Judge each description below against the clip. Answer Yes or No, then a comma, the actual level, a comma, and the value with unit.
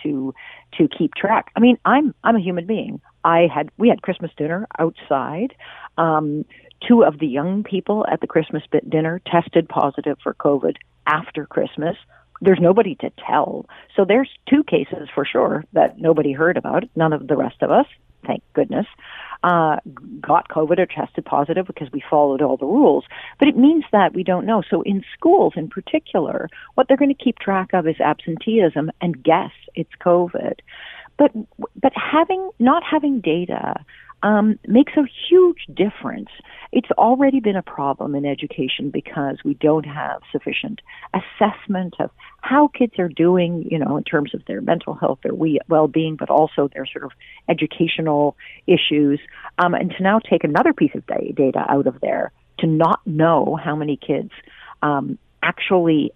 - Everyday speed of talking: Yes, average, 170 wpm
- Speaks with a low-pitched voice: No, medium, 175 Hz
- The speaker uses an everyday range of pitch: No, wide, 6.9 semitones